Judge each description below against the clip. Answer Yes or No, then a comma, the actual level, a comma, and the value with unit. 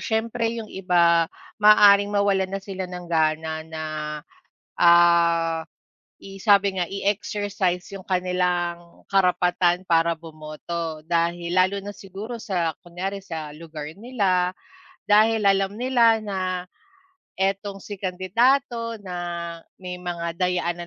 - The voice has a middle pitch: Yes, medium, 180 Hz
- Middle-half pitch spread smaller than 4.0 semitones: Yes, average, 2.8 semitones